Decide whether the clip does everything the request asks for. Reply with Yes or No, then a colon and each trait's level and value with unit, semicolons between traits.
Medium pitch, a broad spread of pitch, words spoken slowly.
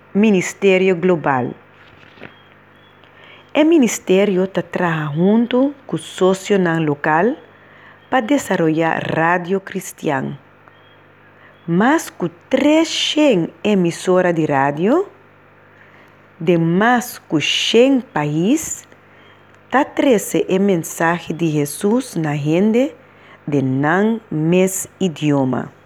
Yes: medium, 180 Hz; wide, 5.7 semitones; slow, 80 wpm